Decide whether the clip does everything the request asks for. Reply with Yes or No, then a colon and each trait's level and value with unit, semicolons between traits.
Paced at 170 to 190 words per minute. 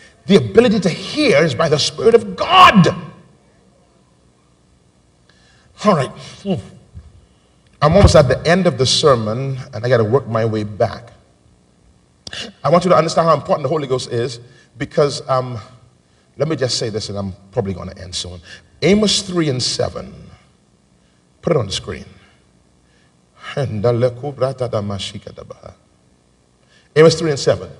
No: average, 140 wpm